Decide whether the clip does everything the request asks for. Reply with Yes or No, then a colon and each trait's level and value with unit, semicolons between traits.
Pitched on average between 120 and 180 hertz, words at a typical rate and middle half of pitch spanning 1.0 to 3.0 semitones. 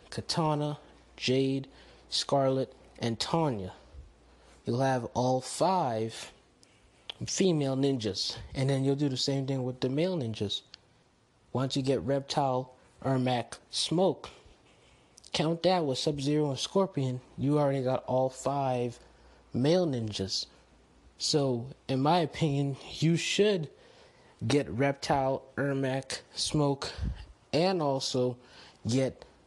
No: low, 135 Hz; slow, 110 wpm; average, 2.7 semitones